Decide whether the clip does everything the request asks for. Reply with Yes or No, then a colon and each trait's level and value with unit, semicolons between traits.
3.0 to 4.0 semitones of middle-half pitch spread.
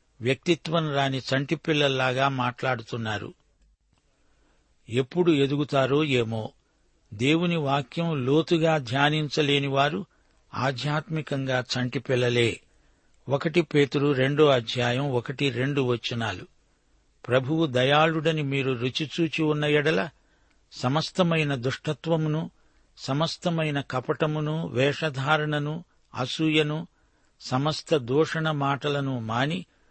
Yes: average, 3.4 semitones